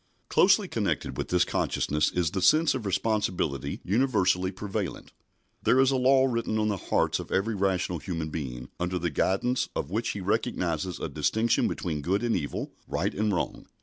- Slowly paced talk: No, average, 180 wpm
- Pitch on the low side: Yes, very low, 95 Hz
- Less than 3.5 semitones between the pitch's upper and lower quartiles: No, average, 4.4 semitones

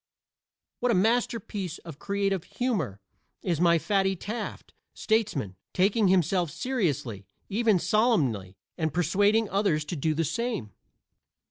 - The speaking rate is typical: No, slow, 120 wpm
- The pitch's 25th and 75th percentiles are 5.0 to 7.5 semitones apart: Yes, wide, 5.5 semitones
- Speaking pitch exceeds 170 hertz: Yes, medium, 185 Hz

